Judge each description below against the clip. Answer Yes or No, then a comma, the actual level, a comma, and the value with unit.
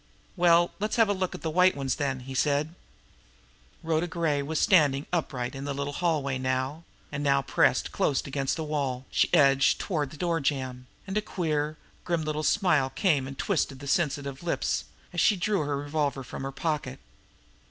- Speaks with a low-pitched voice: No, medium, 150 Hz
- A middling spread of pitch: Yes, average, 3.7 semitones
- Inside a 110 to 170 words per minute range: No, average, 185 wpm